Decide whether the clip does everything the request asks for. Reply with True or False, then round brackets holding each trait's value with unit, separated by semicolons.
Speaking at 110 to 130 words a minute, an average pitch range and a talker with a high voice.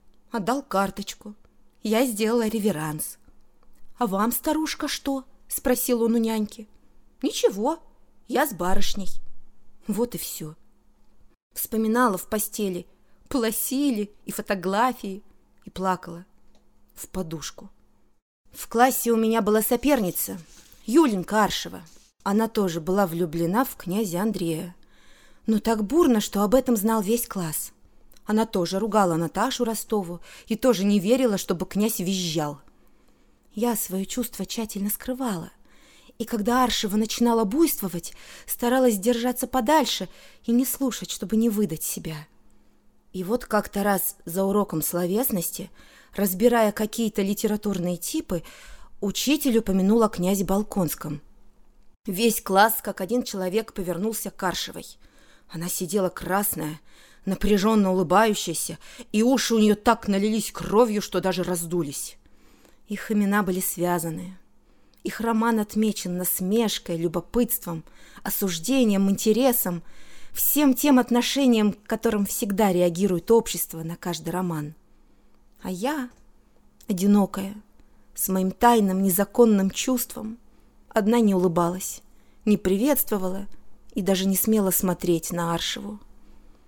True (115 wpm; 4.0 semitones; 205 Hz)